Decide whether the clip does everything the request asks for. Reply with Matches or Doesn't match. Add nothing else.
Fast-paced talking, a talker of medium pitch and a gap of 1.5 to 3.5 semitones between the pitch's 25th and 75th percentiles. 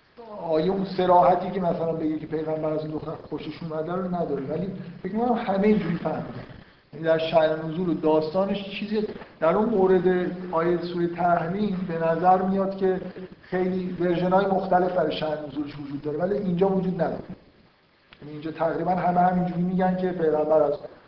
Matches